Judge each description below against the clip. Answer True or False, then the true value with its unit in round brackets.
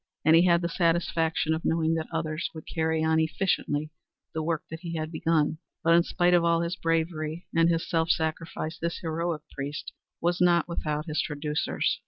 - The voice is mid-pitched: True (165 Hz)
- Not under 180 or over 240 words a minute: True (190 wpm)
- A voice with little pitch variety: True (1.2 semitones)